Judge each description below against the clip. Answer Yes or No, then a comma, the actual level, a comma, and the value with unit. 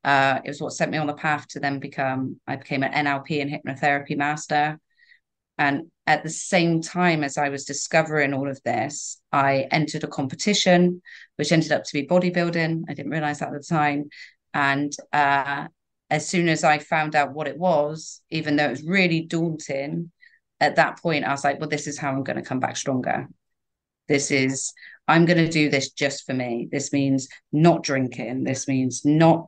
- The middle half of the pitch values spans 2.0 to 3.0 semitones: Yes, narrow, 2.4 semitones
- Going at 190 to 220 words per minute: Yes, average, 200 wpm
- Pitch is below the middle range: No, medium, 150 Hz